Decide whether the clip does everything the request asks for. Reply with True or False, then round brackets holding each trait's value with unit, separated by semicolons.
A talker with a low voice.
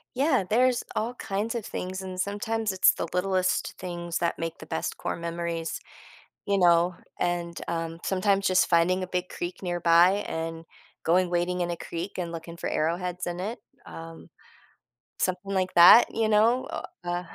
False (180 Hz)